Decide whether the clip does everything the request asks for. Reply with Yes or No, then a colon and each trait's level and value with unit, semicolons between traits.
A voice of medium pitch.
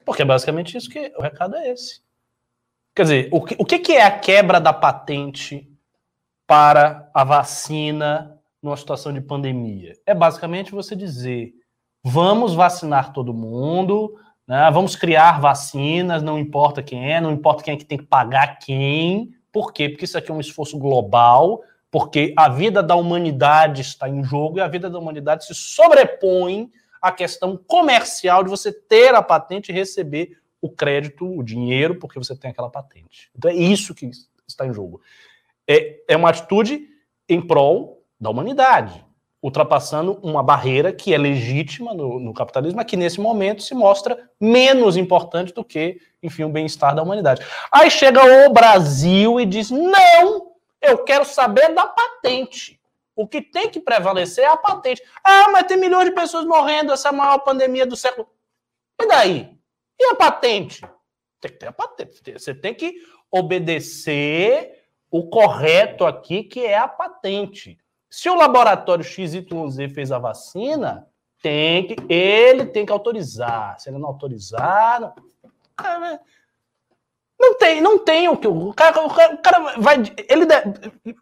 Yes: medium, 180 Hz